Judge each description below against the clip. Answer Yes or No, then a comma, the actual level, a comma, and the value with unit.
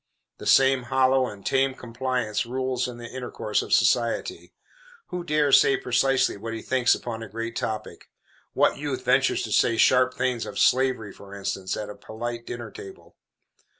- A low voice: Yes, low, 125 Hz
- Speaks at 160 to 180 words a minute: Yes, average, 170 wpm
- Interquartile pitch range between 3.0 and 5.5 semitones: No, narrow, 2.6 semitones